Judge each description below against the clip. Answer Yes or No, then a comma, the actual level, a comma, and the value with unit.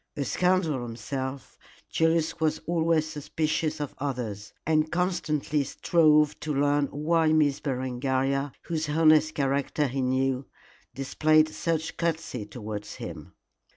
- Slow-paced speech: Yes, slow, 120 wpm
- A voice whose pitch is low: No, medium, 150 Hz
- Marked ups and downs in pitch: No, average, 3.0 semitones